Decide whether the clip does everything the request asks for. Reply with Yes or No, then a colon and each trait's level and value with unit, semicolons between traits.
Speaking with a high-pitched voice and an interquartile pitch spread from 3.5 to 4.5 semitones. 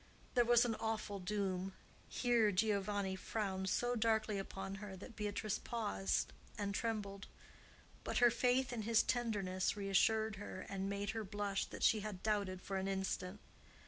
No: high, 205 Hz; narrow, 2.4 semitones